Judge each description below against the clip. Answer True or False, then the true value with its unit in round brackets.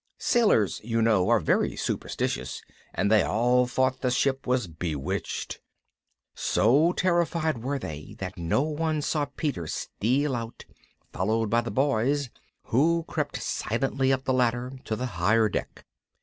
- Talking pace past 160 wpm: False (145 wpm)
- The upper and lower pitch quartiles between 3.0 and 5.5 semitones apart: True (4.5 semitones)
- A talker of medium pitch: False (125 Hz)